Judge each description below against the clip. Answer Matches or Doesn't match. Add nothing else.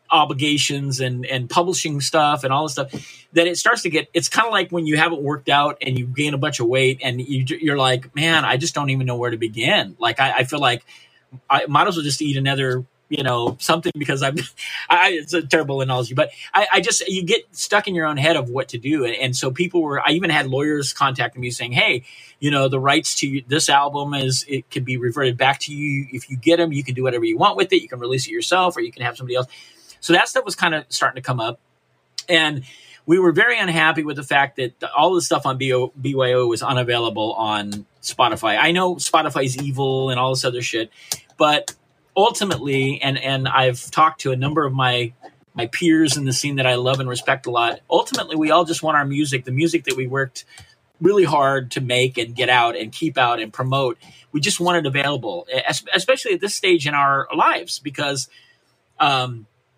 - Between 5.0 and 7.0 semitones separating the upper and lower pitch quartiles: Doesn't match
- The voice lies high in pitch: Doesn't match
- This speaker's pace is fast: Matches